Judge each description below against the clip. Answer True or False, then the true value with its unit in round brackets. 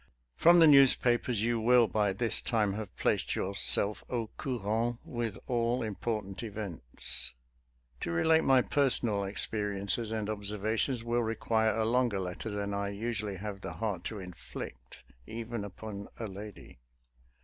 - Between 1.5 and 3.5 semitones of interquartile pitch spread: True (2.8 semitones)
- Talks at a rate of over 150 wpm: False (140 wpm)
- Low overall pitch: True (110 Hz)